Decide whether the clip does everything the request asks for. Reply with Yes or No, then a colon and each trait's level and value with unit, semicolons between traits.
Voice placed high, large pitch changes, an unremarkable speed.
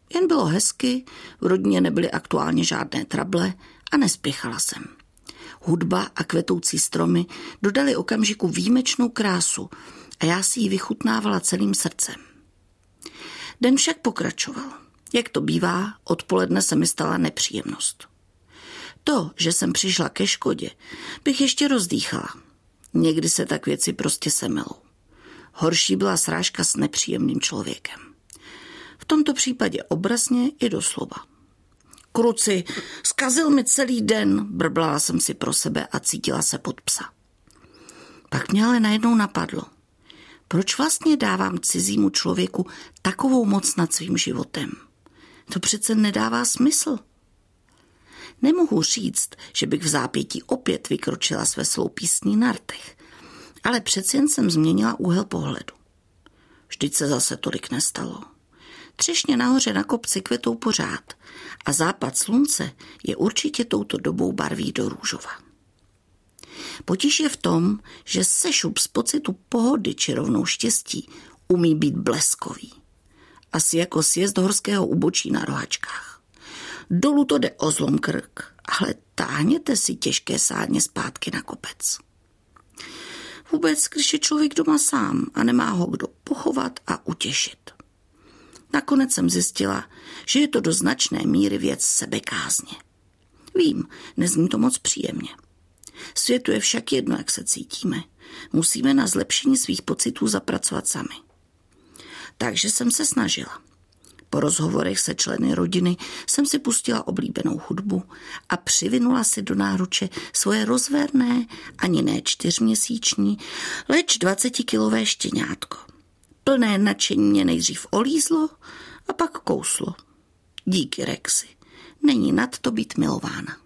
Yes: high, 240 Hz; wide, 8.2 semitones; average, 125 wpm